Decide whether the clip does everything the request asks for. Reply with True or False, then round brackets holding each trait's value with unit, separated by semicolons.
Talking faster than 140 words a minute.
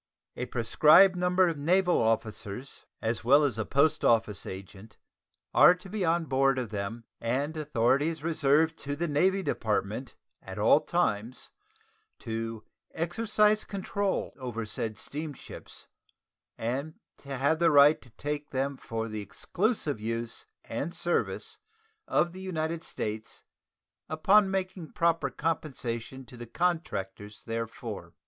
False (135 wpm)